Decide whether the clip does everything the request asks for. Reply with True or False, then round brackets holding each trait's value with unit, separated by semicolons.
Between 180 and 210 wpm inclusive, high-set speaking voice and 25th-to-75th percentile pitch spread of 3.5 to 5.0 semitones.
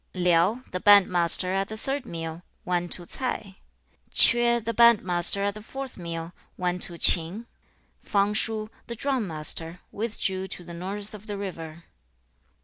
False (165 wpm; 195 Hz; 3.9 semitones)